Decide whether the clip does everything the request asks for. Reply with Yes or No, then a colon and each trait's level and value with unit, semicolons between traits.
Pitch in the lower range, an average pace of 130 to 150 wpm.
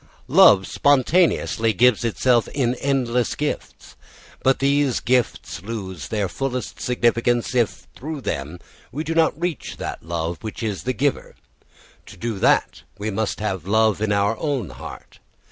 Yes: low, 120 Hz; average, 145 wpm